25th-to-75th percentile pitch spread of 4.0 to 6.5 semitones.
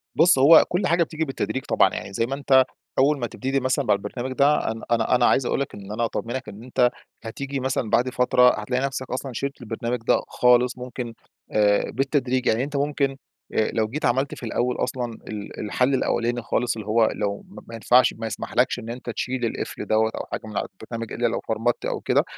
No: average, 2.8 semitones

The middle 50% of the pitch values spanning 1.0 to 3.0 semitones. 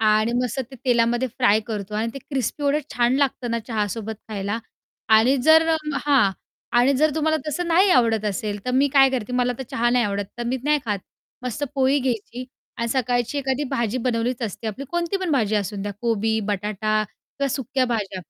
No: average, 4.0 semitones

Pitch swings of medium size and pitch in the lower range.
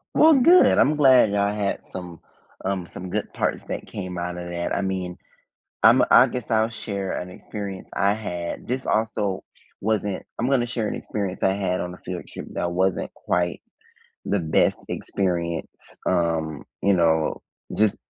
Yes: average, 3.5 semitones; very low, 95 Hz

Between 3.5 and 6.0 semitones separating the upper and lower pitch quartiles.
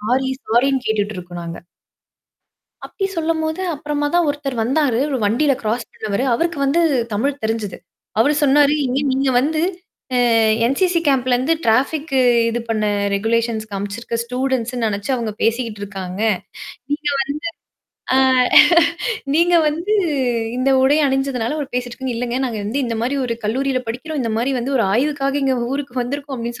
Yes: average, 3.9 semitones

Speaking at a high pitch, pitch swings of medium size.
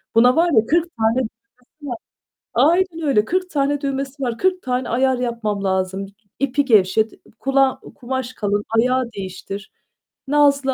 Yes: very high, 255 Hz; average, 4.1 semitones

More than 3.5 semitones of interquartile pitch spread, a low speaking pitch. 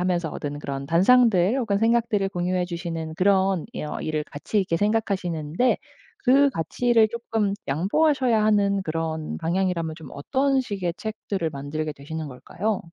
No: average, 5.3 semitones; medium, 185 Hz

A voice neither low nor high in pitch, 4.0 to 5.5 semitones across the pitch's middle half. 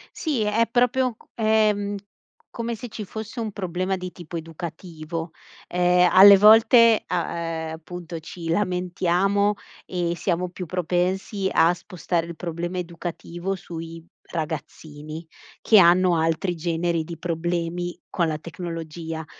No: medium, 175 Hz; average, 2.9 semitones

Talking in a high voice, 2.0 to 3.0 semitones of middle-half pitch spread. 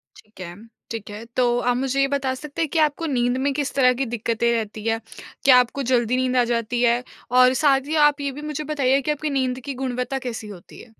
Yes: very high, 255 Hz; average, 2.7 semitones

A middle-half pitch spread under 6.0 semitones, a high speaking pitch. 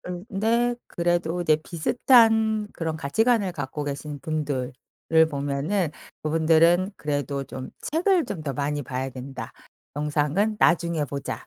No: wide, 5.6 semitones; medium, 160 Hz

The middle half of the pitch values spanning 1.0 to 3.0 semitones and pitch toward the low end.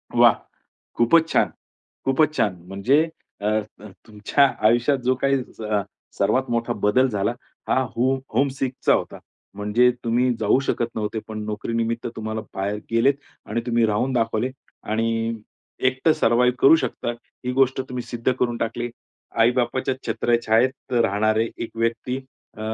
Yes: narrow, 2.5 semitones; low, 120 Hz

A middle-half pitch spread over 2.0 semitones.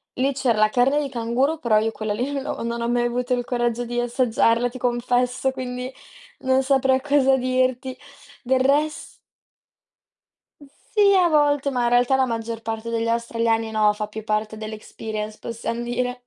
Yes: narrow, 2.4 semitones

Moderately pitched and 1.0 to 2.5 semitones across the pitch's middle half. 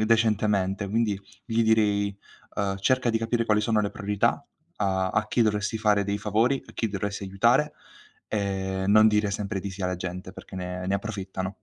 No: low, 105 Hz; narrow, 2.2 semitones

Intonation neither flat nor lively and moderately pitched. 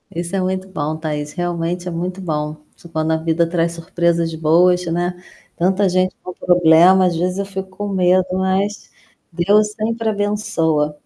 No: narrow, 2.3 semitones; medium, 180 Hz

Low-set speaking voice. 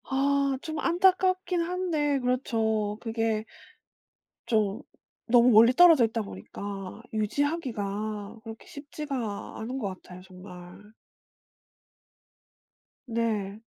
No: high, 230 Hz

